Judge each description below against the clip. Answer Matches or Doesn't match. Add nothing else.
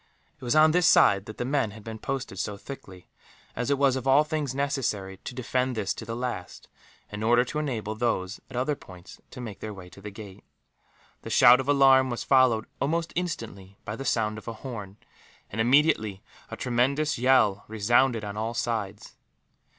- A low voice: Matches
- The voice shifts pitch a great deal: Doesn't match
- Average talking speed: Matches